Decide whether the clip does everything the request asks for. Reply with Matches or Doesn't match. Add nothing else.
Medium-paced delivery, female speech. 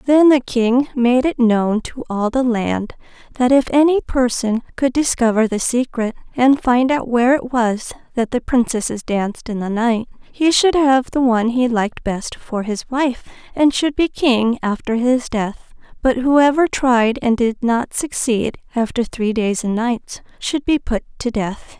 Matches